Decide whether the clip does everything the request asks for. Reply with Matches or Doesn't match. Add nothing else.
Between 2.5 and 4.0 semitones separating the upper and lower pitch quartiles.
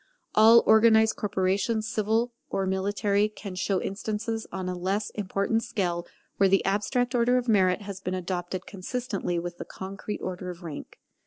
Matches